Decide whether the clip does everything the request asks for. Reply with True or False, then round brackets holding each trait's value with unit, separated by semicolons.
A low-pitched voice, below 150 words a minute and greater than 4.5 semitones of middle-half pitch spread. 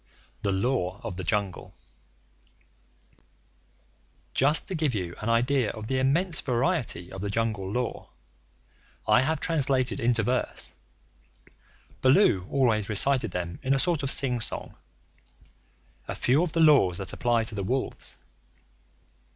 True (120 Hz; 135 wpm; 5.2 semitones)